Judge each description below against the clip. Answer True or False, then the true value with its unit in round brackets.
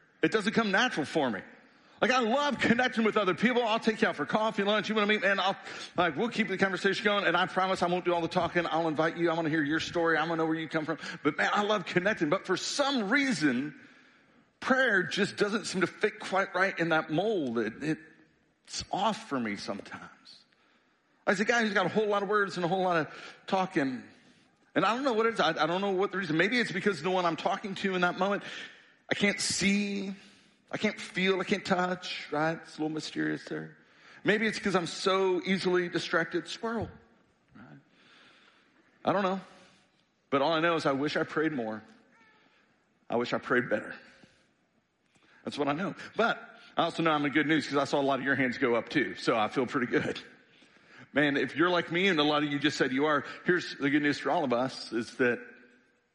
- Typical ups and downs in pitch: True (4.3 semitones)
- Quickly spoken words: True (240 wpm)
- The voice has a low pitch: False (185 Hz)